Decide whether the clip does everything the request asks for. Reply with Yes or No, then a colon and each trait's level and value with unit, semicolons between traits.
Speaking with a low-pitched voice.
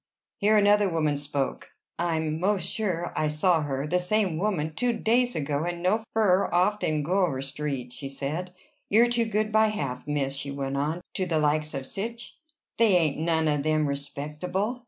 No: medium, 165 Hz